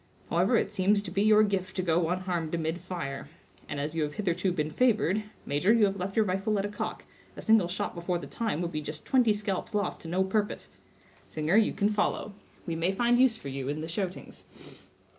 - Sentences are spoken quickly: Yes, fast, 215 wpm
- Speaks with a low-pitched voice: No, medium, 185 Hz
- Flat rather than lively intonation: No, average, 4.1 semitones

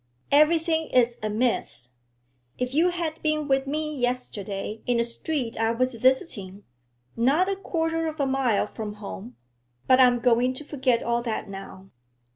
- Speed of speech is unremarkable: Yes, average, 155 wpm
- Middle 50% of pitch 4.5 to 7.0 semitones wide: Yes, average, 5.1 semitones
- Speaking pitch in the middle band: No, very high, 255 Hz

